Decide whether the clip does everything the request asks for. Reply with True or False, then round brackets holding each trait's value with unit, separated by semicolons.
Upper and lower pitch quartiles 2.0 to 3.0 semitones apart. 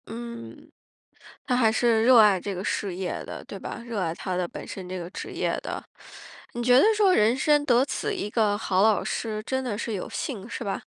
False (3.9 semitones)